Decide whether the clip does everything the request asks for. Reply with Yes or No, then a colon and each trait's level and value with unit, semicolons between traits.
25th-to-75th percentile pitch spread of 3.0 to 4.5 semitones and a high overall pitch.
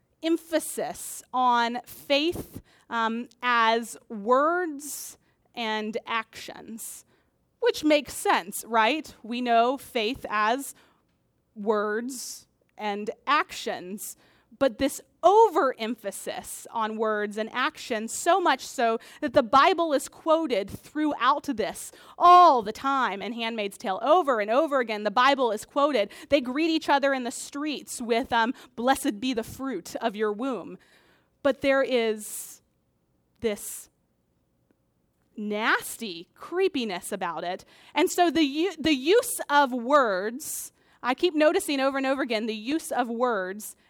No: average, 5.1 semitones; very high, 260 Hz